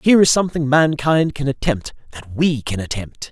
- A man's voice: Yes, male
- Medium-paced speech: Yes, average, 180 wpm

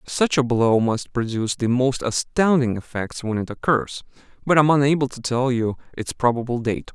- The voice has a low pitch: Yes, low, 125 Hz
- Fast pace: No, average, 190 wpm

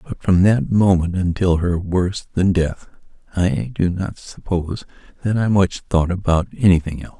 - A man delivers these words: Yes, male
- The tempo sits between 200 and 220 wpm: No, average, 165 wpm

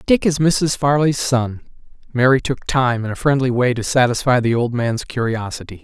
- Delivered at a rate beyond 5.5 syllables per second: No, 5.0 syllables/s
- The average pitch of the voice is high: No, low, 125 Hz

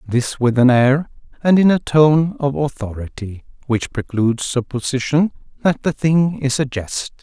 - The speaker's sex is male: Yes, male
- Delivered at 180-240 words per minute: No, average, 160 wpm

